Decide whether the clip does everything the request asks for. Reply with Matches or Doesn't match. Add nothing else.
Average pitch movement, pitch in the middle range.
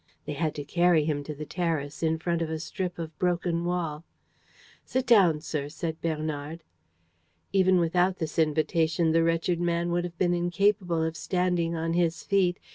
Doesn't match